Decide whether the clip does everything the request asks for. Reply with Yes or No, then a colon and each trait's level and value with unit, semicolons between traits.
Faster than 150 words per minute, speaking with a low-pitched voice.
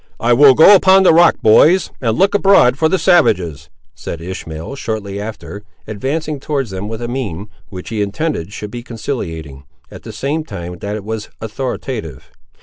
Yes: average, 175 wpm; low, 110 Hz